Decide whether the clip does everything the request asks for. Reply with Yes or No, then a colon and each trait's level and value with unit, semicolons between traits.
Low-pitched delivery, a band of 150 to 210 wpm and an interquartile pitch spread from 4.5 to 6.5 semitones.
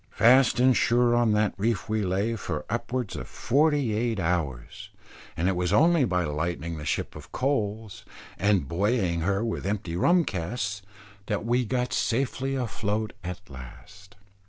Yes: low, 105 Hz; average, 155 wpm; average, 5.3 semitones